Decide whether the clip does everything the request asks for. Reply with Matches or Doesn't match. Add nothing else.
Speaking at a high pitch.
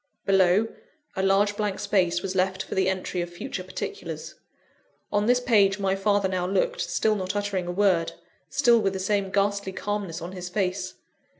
Matches